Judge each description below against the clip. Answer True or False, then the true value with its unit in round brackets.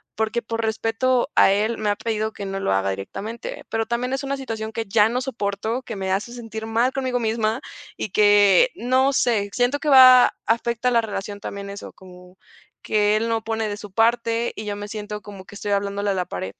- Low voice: False (220 Hz)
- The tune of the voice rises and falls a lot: False (2.7 semitones)